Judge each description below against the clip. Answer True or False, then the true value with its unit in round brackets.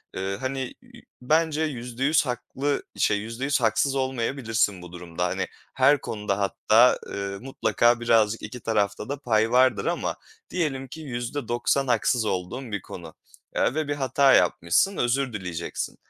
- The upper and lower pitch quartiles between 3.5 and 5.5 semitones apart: True (4.5 semitones)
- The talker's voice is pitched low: True (120 Hz)